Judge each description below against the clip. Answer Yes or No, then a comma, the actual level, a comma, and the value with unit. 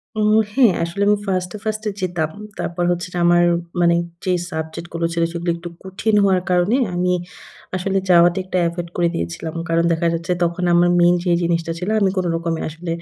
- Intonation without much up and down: Yes, narrow, 1.6 semitones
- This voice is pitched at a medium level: Yes, medium, 175 Hz